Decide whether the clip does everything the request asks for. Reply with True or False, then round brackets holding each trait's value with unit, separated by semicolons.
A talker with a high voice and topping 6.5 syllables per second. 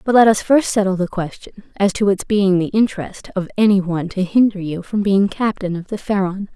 False (195 Hz; 5.5 syllables/s)